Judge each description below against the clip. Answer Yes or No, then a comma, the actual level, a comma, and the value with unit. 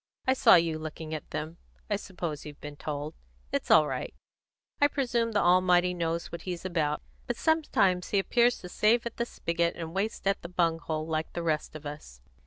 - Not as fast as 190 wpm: No, average, 200 wpm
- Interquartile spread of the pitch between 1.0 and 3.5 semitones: No, average, 4.1 semitones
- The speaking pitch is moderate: Yes, medium, 170 Hz